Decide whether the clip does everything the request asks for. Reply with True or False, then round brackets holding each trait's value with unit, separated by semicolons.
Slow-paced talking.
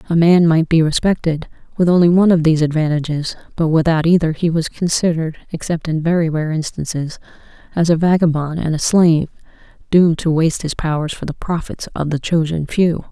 False (185 wpm)